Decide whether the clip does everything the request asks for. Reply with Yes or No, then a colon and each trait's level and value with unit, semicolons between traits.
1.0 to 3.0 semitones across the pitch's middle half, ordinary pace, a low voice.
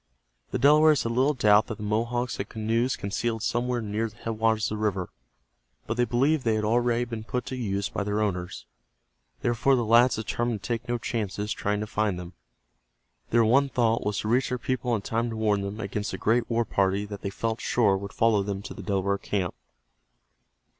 No: narrow, 2.6 semitones; fast, 210 wpm; low, 110 Hz